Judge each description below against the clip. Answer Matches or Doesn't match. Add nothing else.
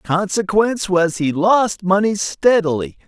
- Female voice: Doesn't match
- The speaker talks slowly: Matches